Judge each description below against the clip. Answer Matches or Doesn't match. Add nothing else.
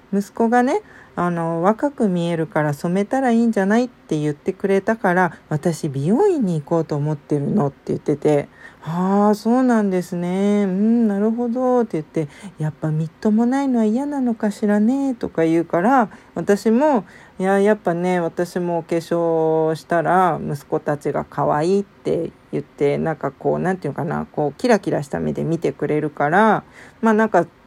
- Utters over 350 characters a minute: Doesn't match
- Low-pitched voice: Doesn't match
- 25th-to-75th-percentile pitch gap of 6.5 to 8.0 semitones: Doesn't match